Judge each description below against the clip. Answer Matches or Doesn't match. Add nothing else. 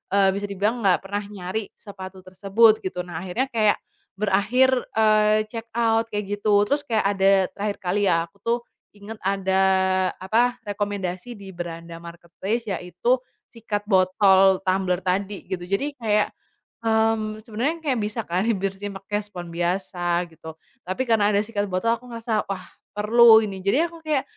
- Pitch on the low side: Doesn't match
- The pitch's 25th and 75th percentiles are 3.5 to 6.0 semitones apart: Doesn't match